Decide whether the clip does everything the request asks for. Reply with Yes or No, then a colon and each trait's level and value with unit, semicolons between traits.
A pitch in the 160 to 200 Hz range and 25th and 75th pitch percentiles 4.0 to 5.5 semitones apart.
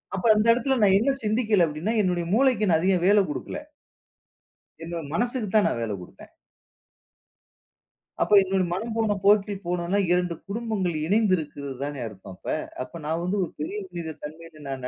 Yes: medium, 185 Hz; average, 4.7 semitones